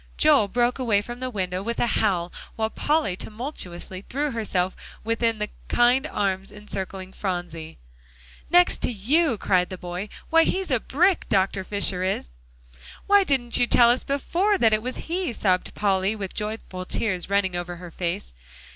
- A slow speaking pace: No, average, 165 wpm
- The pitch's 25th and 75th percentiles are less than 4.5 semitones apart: No, average, 5.0 semitones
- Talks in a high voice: Yes, high, 210 Hz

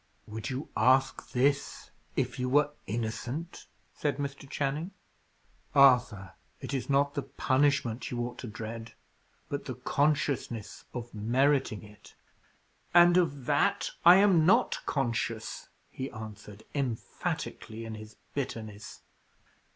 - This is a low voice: Yes, low, 130 Hz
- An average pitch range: Yes, average, 4.2 semitones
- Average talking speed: No, slow, 120 wpm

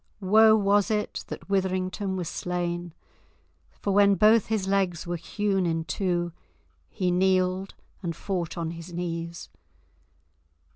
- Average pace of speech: No, slow, 130 wpm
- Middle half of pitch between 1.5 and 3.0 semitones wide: Yes, narrow, 2.4 semitones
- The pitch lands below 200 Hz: Yes, medium, 185 Hz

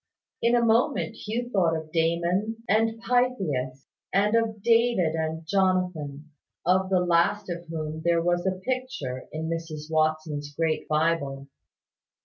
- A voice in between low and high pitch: Yes, medium, 170 Hz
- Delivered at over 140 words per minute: No, slow, 135 wpm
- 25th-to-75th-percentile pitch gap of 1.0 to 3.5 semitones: No, average, 5.3 semitones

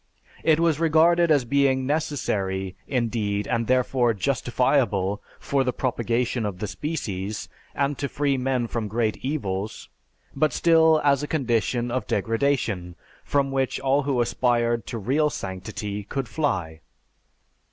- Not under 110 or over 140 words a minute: Yes, slow, 135 wpm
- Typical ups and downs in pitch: Yes, average, 4.6 semitones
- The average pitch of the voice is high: No, low, 125 Hz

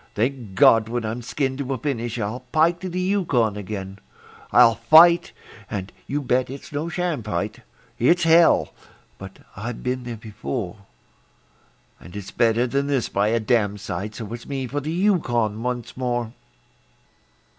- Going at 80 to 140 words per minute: No, average, 155 wpm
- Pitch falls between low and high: No, low, 120 Hz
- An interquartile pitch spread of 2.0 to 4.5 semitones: No, average, 4.9 semitones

